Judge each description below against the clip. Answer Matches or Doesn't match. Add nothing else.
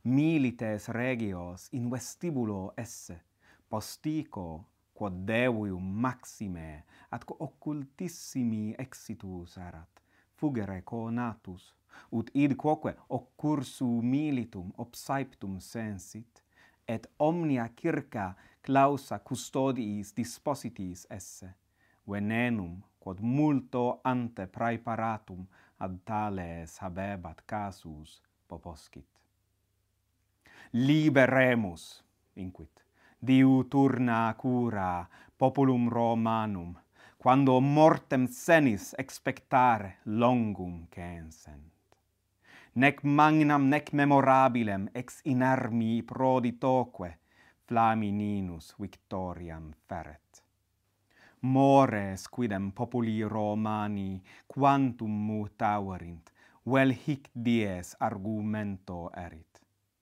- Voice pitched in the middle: Doesn't match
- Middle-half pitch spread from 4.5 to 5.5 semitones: Matches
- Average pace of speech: Doesn't match